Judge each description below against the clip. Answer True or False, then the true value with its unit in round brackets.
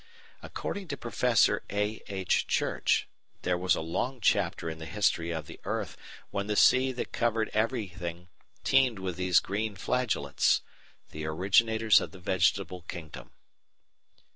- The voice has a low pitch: True (100 Hz)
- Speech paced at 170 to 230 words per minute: False (140 wpm)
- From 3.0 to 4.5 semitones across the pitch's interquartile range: True (4.2 semitones)